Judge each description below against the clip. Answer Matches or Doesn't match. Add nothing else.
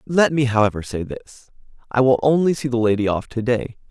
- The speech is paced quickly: Matches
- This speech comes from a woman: Doesn't match